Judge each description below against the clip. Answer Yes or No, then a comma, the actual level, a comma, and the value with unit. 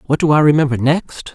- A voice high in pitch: No, medium, 145 Hz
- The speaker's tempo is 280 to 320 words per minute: No, fast, 225 wpm